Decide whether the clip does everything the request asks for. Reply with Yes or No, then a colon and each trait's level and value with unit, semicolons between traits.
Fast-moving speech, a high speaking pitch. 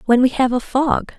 Yes: fast, 250 wpm; very high, 255 Hz